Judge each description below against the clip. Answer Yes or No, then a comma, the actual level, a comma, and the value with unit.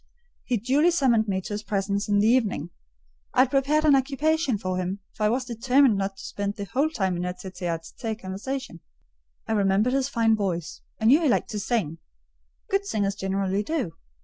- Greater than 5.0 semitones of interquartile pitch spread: Yes, wide, 5.4 semitones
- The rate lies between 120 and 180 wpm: No, average, 200 wpm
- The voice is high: Yes, high, 215 Hz